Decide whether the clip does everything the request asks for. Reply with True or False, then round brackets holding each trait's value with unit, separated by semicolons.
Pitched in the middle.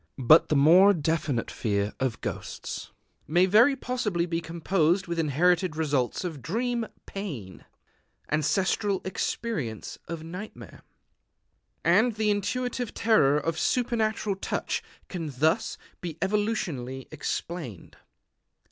True (175 Hz)